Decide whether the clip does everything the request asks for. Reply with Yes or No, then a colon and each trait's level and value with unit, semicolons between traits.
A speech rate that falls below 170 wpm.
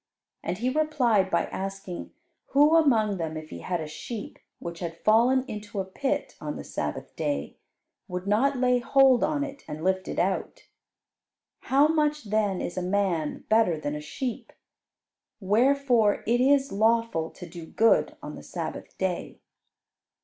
Yes: average, 160 wpm